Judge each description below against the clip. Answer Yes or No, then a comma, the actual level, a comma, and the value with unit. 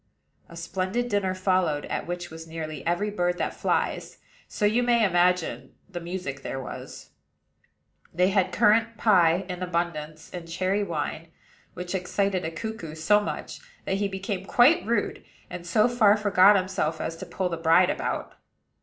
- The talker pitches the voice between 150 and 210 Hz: Yes, medium, 185 Hz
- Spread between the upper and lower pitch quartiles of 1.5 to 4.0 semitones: Yes, average, 3.3 semitones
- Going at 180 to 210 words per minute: No, average, 165 wpm